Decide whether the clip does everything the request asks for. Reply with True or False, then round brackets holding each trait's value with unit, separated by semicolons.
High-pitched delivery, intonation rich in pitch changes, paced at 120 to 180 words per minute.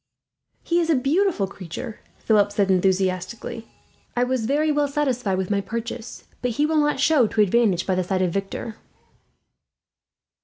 True (225 Hz; 6.4 semitones; 160 wpm)